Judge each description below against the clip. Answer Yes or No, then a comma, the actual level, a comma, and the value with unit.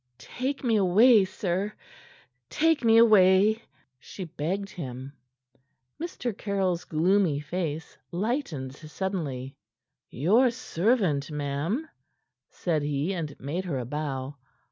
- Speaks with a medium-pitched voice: Yes, medium, 180 Hz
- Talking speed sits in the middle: No, slow, 105 wpm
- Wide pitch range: Yes, wide, 6.4 semitones